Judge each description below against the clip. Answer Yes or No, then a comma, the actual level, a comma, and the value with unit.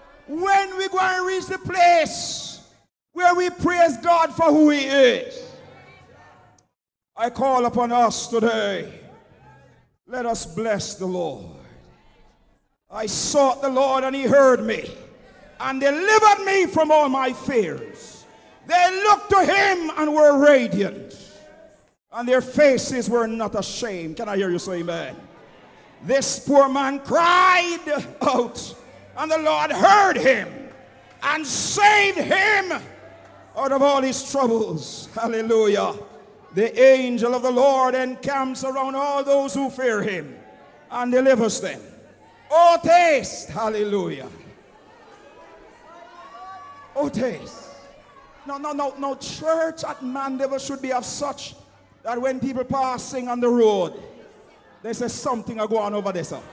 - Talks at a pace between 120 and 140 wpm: Yes, slow, 135 wpm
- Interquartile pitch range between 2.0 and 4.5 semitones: No, average, 5.2 semitones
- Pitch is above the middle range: Yes, very high, 270 Hz